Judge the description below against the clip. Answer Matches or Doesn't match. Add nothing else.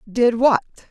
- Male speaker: Doesn't match